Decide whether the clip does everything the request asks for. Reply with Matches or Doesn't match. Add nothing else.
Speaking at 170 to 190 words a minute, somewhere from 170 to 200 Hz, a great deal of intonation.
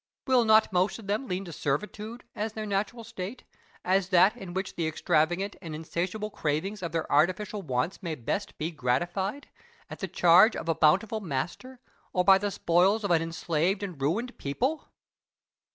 Doesn't match